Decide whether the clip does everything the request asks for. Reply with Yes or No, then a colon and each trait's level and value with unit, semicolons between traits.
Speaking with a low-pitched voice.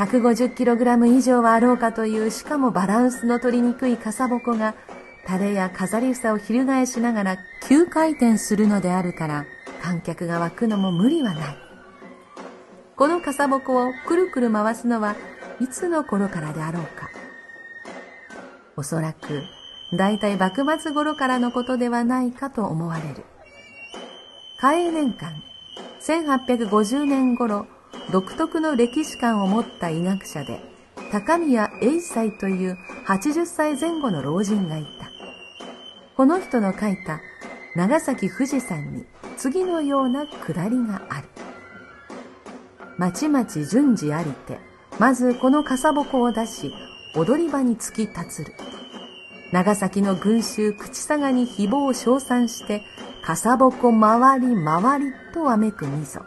No: high, 235 Hz